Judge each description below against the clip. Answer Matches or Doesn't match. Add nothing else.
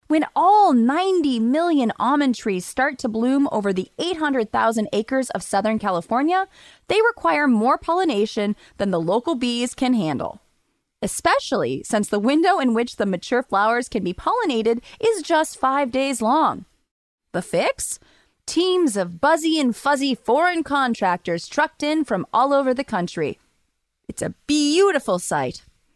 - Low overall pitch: Doesn't match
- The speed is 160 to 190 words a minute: Doesn't match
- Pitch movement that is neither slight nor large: Doesn't match